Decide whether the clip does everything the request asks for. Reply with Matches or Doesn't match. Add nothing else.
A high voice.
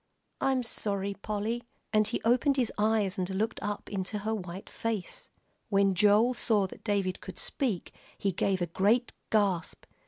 Matches